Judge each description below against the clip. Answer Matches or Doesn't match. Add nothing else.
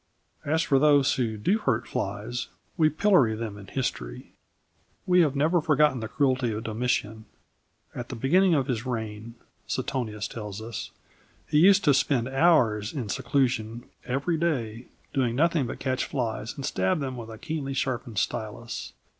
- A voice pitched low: Matches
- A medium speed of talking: Matches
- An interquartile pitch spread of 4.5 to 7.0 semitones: Matches